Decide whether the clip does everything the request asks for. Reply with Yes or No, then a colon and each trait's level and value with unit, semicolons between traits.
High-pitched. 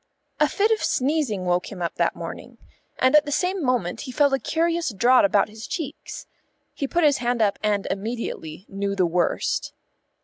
Yes: high, 240 Hz